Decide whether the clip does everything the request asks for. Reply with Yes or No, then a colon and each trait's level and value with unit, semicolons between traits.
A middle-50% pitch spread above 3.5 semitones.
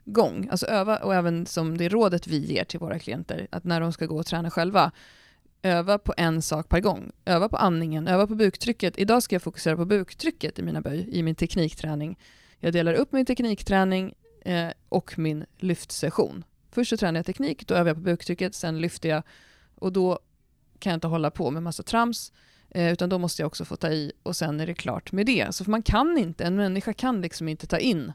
No: average, 3.2 semitones